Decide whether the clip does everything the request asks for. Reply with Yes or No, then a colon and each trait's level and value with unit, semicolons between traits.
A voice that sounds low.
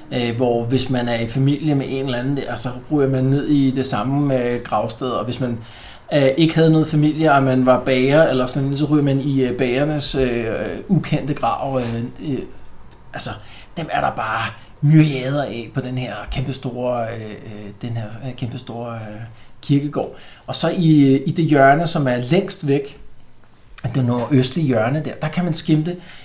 Yes: low, 130 Hz